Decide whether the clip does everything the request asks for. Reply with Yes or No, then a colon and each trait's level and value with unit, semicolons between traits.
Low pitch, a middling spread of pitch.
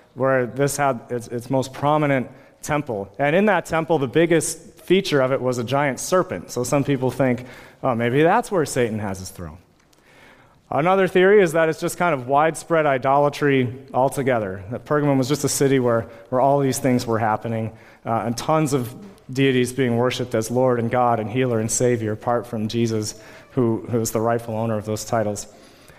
Yes: low, 130 Hz; average, 3.8 semitones